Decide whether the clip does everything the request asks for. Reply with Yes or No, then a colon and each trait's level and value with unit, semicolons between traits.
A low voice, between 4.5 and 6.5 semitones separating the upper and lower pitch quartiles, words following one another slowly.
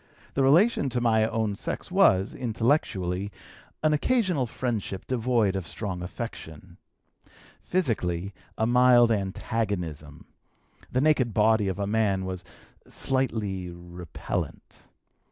Yes: low, 110 Hz; average, 4.9 semitones; slow, 110 wpm